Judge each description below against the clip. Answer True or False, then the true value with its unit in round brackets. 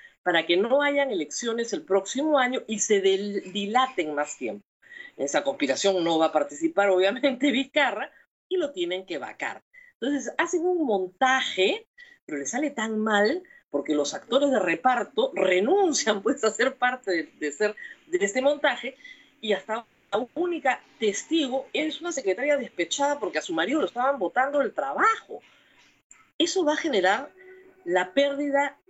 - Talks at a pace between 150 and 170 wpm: True (160 wpm)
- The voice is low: False (260 Hz)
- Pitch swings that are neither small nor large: False (6.8 semitones)